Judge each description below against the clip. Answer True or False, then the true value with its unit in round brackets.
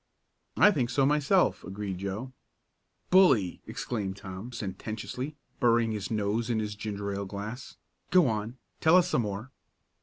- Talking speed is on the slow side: False (145 wpm)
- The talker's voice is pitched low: True (110 Hz)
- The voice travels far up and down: False (4.2 semitones)